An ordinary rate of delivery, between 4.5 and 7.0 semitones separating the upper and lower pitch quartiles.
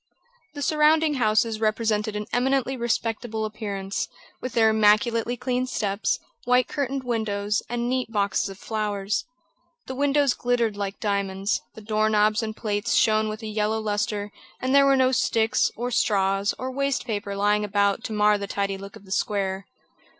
No: average, 165 wpm; average, 3.1 semitones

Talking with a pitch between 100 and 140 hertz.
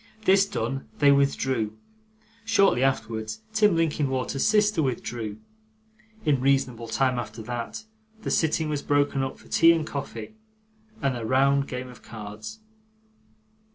Yes: low, 135 Hz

